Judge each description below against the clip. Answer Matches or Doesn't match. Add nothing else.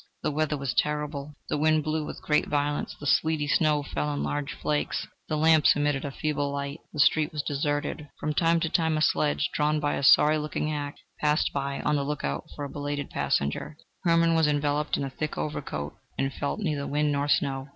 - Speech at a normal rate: Doesn't match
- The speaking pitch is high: Doesn't match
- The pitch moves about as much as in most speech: Doesn't match